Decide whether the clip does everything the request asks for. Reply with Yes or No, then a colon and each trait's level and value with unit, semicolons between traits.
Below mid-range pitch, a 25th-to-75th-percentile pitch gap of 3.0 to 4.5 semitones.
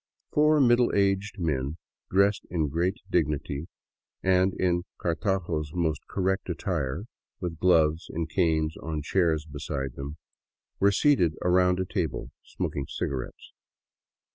Yes: very low, 85 Hz; average, 3.7 semitones